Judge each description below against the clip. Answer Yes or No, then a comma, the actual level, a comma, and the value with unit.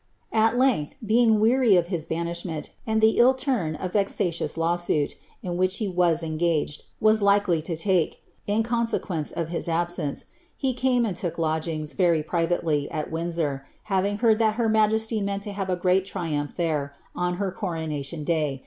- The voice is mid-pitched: Yes, medium, 175 Hz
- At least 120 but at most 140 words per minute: No, average, 175 wpm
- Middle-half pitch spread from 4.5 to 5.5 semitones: Yes, average, 4.8 semitones